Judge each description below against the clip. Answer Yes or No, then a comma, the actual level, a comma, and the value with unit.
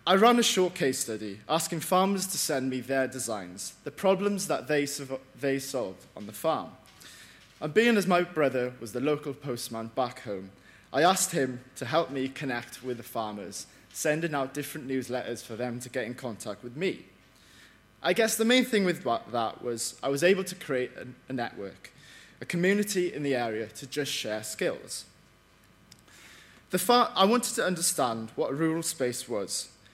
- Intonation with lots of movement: Yes, wide, 6.3 semitones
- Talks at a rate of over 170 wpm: Yes, average, 185 wpm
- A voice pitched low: Yes, low, 130 Hz